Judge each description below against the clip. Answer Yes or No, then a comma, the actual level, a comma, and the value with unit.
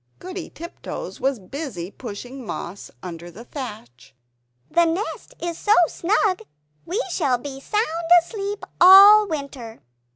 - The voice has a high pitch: Yes, very high, 290 Hz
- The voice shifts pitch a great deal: Yes, wide, 8.3 semitones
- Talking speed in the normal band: No, slow, 125 wpm